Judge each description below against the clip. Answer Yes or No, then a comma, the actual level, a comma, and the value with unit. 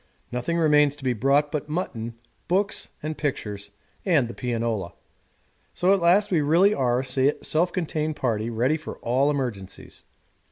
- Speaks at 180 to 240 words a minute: No, average, 155 wpm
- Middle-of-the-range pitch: Yes, medium, 145 Hz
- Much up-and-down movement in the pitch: No, average, 5.0 semitones